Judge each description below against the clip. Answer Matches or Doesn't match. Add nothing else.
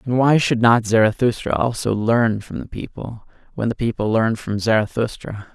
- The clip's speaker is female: Doesn't match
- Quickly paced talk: Doesn't match